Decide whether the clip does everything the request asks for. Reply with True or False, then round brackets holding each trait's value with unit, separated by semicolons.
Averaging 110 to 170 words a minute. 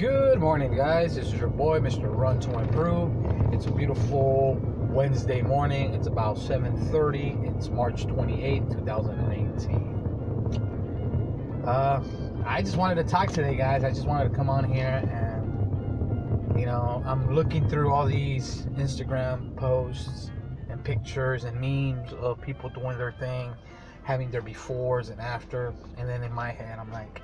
True (160 wpm)